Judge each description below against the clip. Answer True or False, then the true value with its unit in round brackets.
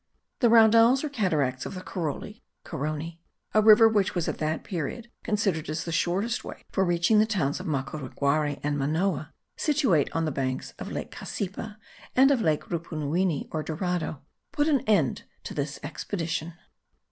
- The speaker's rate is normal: True (165 wpm)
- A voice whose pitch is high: False (170 Hz)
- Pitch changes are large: True (5.9 semitones)